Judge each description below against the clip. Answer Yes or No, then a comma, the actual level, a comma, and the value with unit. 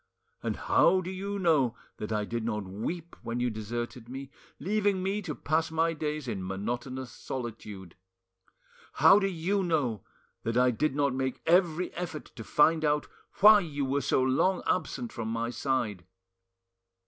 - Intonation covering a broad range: Yes, wide, 6.4 semitones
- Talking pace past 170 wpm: No, average, 160 wpm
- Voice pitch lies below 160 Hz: Yes, low, 135 Hz